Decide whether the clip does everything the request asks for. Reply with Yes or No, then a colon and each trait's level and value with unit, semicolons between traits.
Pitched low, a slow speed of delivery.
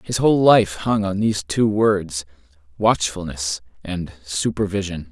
Yes: very low, 95 Hz; slow, 130 wpm